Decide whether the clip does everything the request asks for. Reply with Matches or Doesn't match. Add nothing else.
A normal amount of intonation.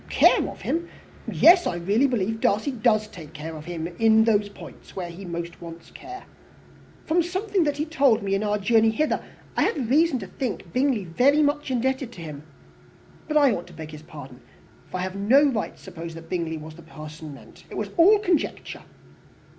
Doesn't match